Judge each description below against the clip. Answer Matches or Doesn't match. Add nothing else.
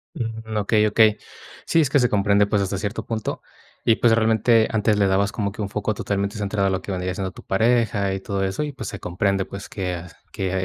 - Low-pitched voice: Matches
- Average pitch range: Doesn't match